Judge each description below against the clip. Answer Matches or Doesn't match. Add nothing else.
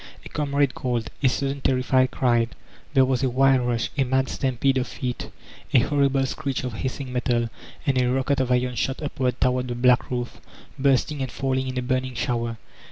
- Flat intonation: Matches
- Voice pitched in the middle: Doesn't match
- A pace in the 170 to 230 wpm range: Matches